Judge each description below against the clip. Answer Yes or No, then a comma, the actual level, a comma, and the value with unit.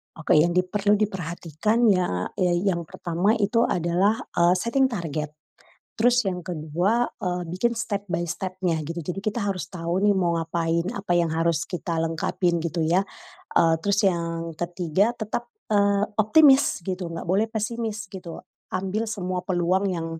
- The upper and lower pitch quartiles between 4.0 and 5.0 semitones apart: No, average, 3.4 semitones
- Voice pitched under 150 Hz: No, medium, 180 Hz